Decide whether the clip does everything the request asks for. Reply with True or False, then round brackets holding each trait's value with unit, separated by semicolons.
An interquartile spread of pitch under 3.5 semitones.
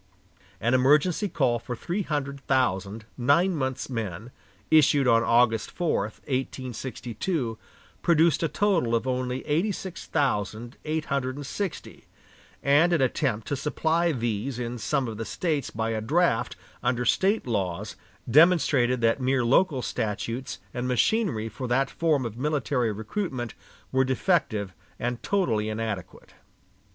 False (4.9 semitones)